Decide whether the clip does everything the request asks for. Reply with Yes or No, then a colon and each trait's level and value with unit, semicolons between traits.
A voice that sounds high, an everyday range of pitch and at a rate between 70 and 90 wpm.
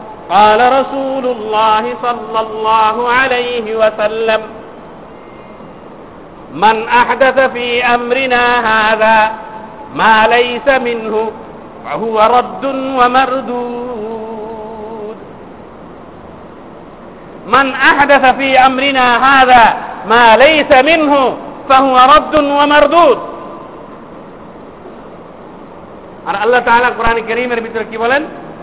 Yes: high, 245 Hz; average, 3.3 semitones; average, 75 wpm